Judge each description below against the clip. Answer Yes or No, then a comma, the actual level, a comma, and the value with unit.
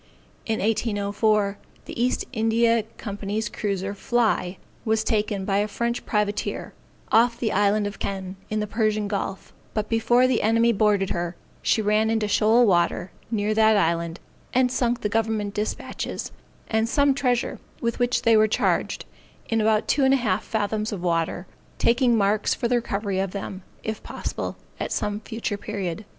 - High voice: Yes, high, 215 Hz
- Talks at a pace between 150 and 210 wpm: Yes, average, 165 wpm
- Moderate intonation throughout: No, narrow, 2.2 semitones